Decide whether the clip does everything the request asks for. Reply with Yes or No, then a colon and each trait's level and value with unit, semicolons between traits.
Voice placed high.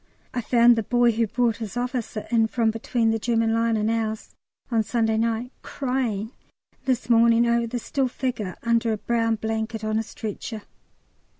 Yes: high, 230 Hz